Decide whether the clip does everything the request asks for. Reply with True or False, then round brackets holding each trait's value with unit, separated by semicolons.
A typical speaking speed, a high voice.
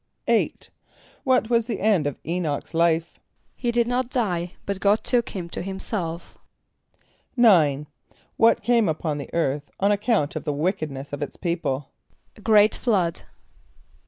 False (155 wpm; 180 Hz)